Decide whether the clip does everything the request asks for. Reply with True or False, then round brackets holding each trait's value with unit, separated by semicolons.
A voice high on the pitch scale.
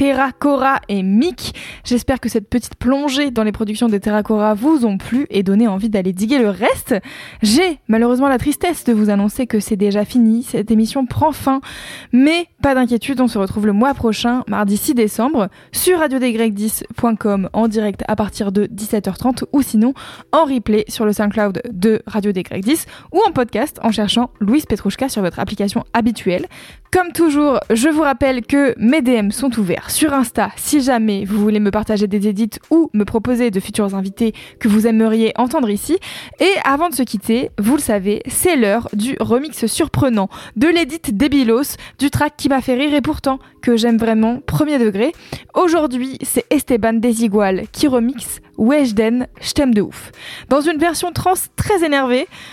True (235 Hz)